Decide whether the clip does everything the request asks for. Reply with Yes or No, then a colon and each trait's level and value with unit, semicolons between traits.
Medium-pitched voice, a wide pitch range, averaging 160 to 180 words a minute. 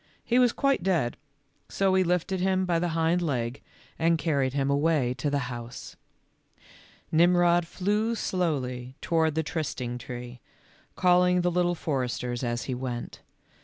No: medium, 160 Hz; wide, 5.9 semitones; average, 145 wpm